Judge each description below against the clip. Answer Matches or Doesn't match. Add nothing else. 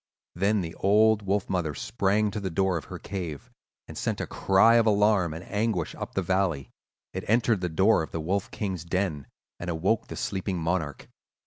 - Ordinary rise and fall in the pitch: Matches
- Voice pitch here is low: Matches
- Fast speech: Doesn't match